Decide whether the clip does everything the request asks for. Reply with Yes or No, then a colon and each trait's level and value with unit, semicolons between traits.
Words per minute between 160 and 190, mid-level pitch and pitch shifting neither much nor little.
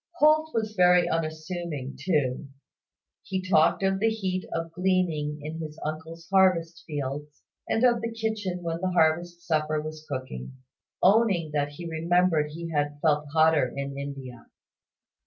No: average, 145 wpm; medium, 165 Hz; average, 3.6 semitones